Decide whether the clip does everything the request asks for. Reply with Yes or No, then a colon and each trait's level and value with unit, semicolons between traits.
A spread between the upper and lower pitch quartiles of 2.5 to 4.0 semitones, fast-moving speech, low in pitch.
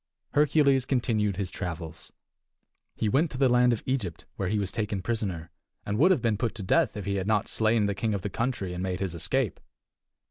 No: average, 4.5 semitones; fast, 215 wpm; low, 105 Hz